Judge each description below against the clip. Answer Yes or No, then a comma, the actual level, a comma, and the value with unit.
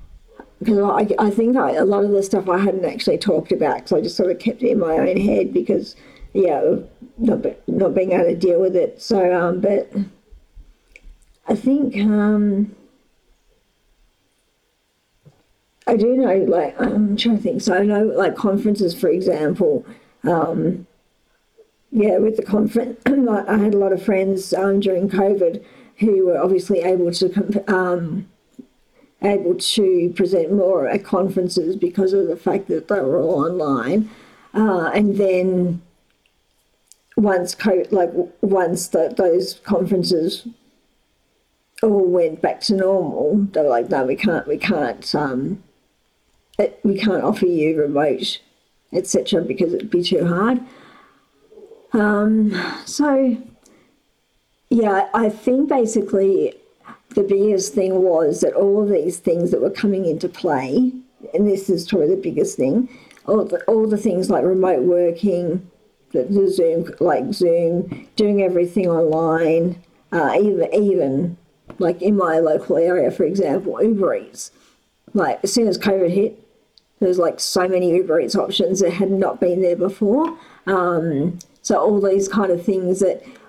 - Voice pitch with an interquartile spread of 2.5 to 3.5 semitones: Yes, average, 3.2 semitones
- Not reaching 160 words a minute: Yes, average, 150 wpm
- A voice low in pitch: No, high, 195 Hz